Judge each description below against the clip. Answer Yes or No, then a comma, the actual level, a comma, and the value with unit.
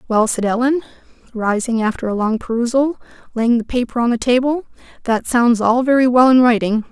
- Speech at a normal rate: Yes, average, 180 wpm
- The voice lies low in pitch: No, high, 240 Hz